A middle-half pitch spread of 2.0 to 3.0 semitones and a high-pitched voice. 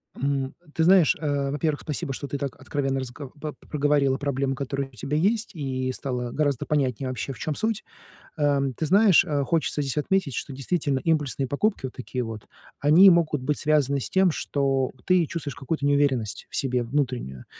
No: narrow, 2.6 semitones; medium, 140 Hz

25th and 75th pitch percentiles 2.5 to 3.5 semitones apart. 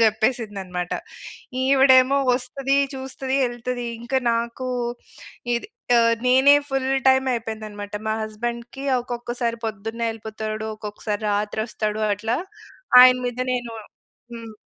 Yes: average, 2.8 semitones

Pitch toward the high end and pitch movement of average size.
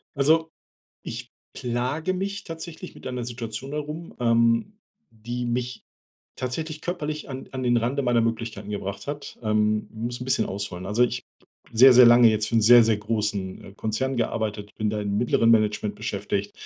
No: low, 120 Hz; average, 3.8 semitones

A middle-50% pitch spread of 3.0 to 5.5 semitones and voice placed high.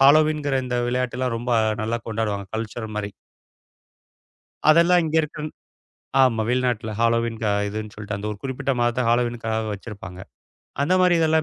No: average, 4.2 semitones; low, 120 Hz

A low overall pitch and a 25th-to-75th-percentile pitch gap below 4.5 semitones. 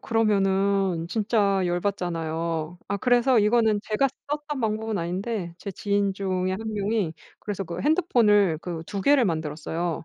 No: high, 200 Hz; average, 4.0 semitones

